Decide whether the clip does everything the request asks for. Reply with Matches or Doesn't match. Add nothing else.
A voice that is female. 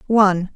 Matches